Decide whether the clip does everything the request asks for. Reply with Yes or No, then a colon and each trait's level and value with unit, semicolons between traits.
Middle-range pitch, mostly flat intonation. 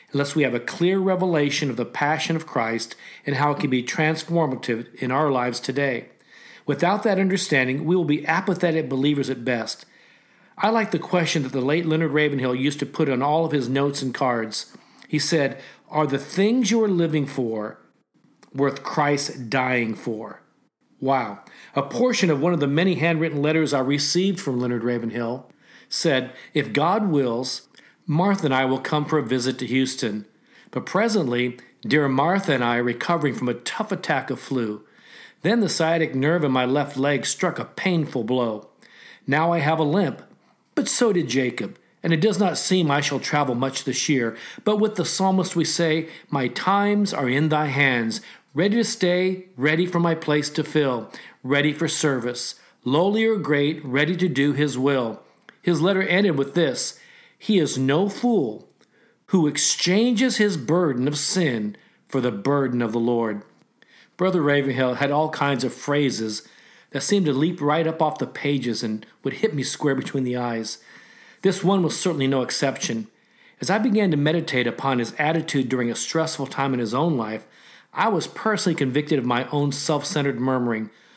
No: medium, 145 Hz; average, 4.8 semitones